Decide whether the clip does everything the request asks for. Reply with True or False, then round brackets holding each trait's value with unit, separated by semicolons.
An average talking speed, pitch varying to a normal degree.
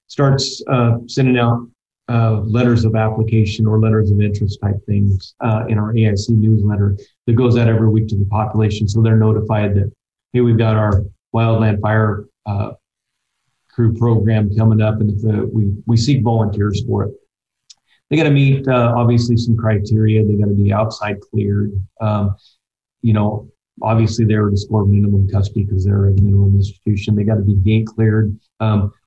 False (180 wpm; 1.7 semitones)